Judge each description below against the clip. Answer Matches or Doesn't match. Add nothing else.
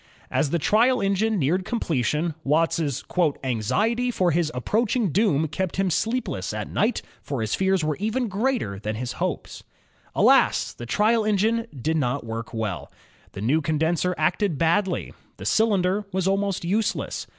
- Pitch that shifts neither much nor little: Doesn't match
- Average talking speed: Matches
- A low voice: Doesn't match